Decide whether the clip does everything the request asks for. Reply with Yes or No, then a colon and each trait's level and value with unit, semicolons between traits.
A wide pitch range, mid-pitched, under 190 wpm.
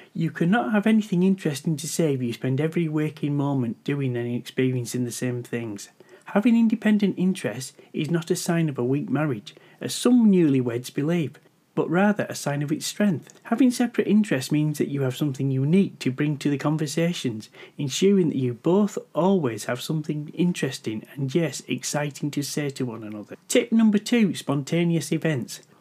Yes: wide, 5.8 semitones; medium, 155 Hz; average, 175 wpm